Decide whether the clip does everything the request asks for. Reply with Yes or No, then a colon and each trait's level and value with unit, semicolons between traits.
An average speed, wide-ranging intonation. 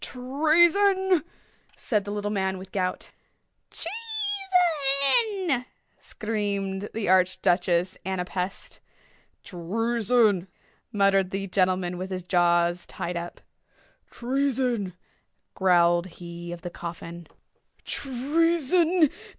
No: slow, 95 wpm; wide, 7.6 semitones